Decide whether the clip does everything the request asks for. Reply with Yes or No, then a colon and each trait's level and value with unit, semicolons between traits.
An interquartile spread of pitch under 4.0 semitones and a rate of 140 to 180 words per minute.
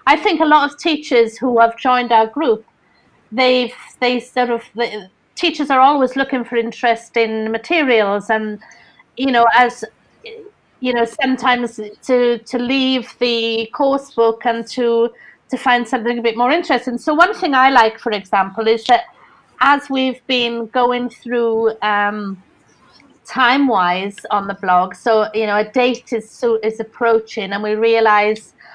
Yes: narrow, 2.6 semitones; average, 165 wpm